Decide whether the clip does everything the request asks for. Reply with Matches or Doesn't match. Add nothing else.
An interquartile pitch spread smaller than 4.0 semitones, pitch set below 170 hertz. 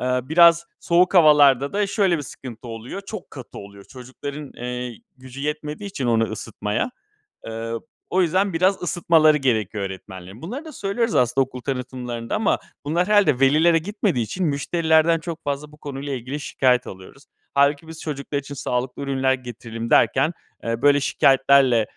Doesn't match